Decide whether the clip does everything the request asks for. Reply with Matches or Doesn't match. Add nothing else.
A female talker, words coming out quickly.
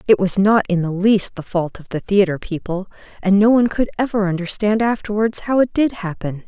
Matches